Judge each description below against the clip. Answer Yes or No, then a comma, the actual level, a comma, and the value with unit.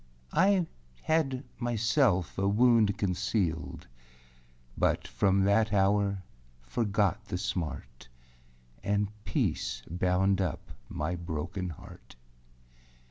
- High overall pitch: No, low, 100 Hz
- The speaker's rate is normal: No, slow, 90 wpm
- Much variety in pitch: No, average, 3.7 semitones